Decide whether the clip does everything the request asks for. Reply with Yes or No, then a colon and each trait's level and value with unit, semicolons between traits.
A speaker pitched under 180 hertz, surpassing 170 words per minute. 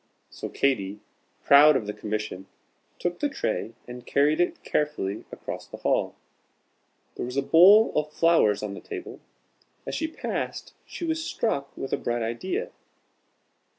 No: medium, 140 Hz; average, 150 wpm